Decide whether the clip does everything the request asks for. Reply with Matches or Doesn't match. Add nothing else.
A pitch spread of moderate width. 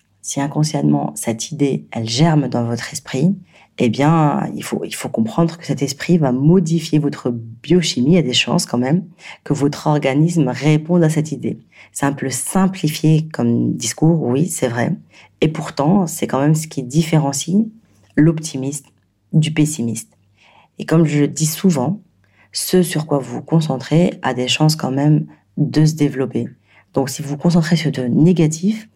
Matches